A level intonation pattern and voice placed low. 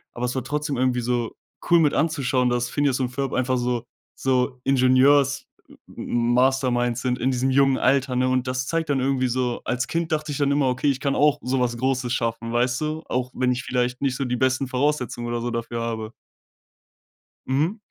Yes: narrow, 2.0 semitones; low, 130 Hz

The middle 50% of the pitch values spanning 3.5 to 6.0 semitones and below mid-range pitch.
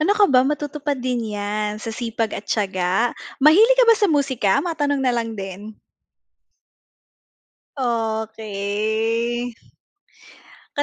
No: average, 5.0 semitones; high, 230 Hz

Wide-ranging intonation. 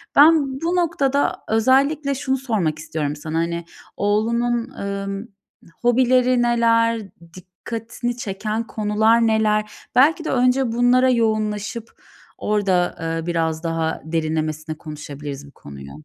Yes: wide, 6.7 semitones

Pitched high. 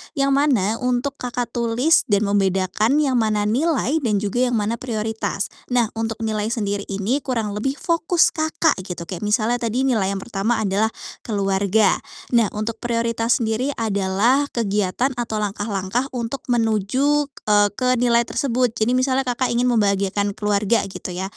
Yes: high, 225 Hz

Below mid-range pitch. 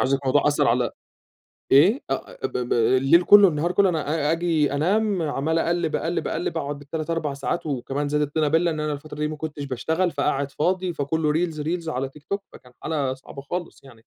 No: medium, 150 Hz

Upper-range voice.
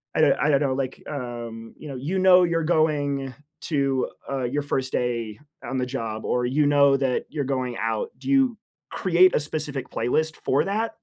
No: medium, 140 Hz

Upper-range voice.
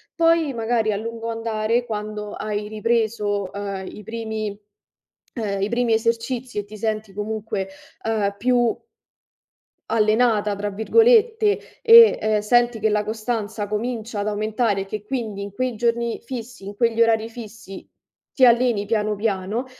Yes: high, 220 Hz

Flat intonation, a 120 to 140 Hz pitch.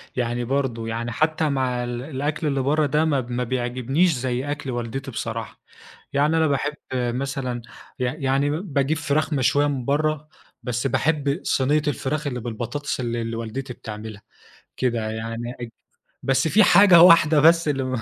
No: average, 3.5 semitones; low, 135 Hz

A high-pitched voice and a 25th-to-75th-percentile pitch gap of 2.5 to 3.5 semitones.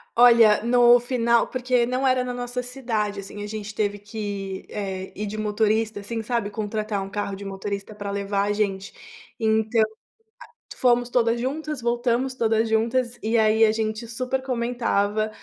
Yes: high, 220 Hz; average, 2.8 semitones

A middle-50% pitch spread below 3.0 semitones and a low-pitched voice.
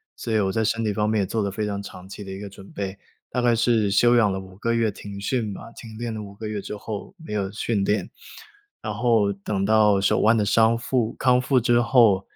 Yes: narrow, 2.6 semitones; low, 105 Hz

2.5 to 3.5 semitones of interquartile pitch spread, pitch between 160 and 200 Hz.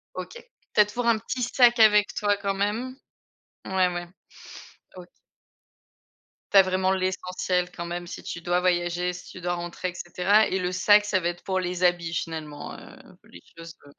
Yes: average, 2.8 semitones; medium, 185 Hz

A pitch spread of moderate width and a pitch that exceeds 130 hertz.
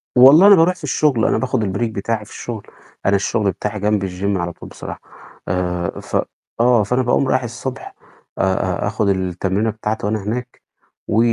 No: average, 3.9 semitones; low, 110 Hz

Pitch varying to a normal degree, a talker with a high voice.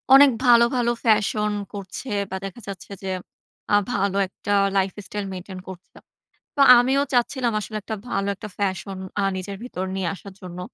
Yes: average, 3.7 semitones; high, 200 Hz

